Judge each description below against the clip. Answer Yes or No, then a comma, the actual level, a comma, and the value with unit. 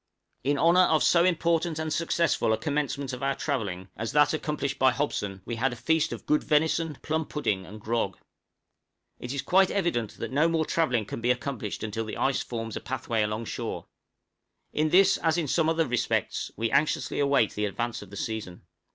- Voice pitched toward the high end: No, medium, 140 Hz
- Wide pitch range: Yes, wide, 5.9 semitones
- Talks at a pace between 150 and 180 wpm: No, average, 195 wpm